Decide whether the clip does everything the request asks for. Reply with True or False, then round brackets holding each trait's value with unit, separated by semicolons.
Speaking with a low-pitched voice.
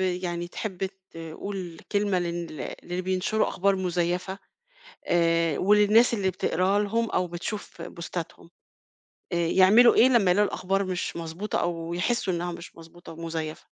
False (180 Hz)